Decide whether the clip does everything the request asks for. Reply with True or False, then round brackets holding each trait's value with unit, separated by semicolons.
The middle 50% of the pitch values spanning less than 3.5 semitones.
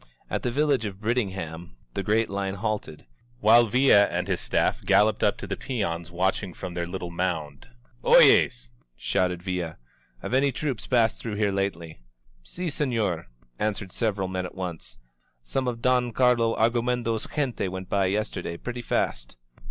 False (4.9 semitones)